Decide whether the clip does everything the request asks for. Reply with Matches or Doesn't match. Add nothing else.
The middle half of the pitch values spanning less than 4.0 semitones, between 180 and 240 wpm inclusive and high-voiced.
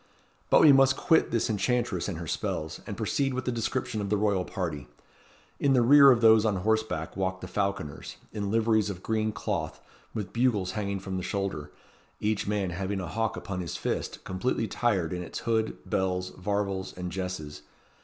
Doesn't match